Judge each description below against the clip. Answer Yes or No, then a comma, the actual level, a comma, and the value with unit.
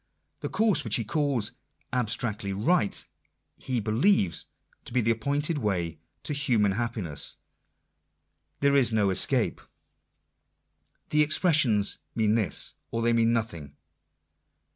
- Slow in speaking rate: Yes, slow, 120 wpm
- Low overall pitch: Yes, low, 115 Hz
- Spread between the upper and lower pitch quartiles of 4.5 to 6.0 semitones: Yes, average, 5.3 semitones